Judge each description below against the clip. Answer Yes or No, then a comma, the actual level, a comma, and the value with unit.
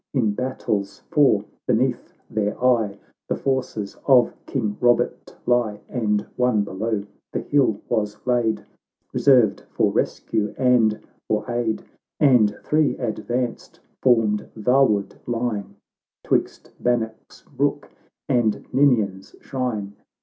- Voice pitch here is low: Yes, low, 115 Hz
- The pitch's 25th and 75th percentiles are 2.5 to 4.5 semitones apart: Yes, average, 3.0 semitones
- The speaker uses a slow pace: Yes, slow, 110 wpm